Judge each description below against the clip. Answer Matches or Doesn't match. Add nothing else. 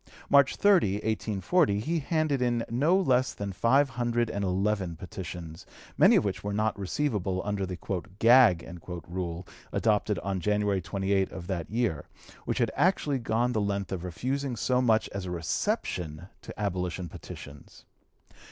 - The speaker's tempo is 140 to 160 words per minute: Matches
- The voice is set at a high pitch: Doesn't match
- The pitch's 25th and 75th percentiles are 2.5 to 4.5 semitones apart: Doesn't match